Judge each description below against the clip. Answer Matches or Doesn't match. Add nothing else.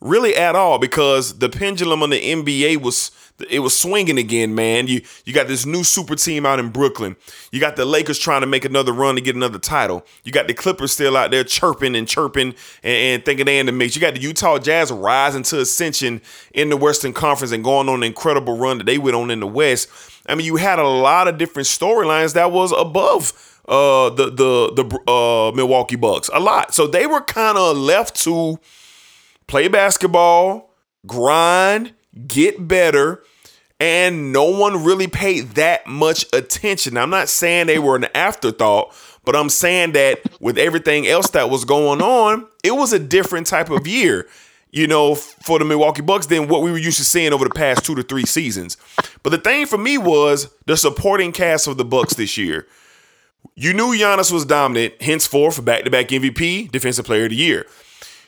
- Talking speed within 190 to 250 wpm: Matches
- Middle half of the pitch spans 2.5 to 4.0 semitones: Doesn't match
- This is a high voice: Doesn't match